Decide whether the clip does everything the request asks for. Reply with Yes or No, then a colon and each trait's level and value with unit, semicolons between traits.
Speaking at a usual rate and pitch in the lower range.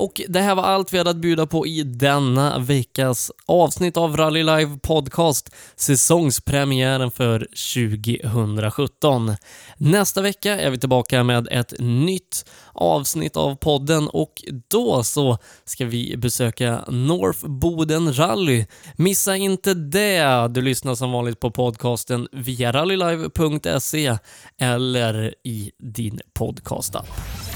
No: slow, 120 wpm; low, 130 Hz